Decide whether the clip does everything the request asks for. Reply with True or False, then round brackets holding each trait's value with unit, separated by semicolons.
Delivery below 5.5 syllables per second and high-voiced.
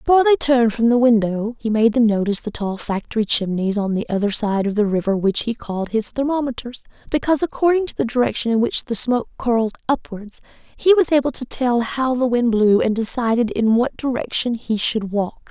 False (5.8 syllables/s; 235 Hz)